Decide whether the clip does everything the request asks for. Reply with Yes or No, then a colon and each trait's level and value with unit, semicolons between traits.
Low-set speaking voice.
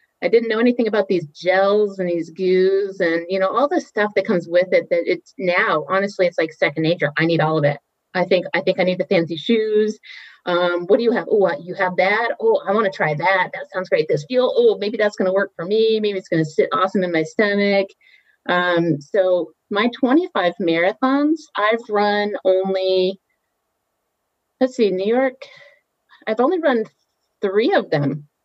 No: high, 195 Hz